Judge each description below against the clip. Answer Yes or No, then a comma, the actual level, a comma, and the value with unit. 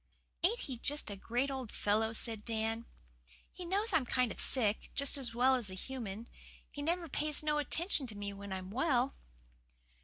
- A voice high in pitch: Yes, very high, 250 Hz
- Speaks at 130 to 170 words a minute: No, average, 185 wpm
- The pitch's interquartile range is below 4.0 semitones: No, average, 4.9 semitones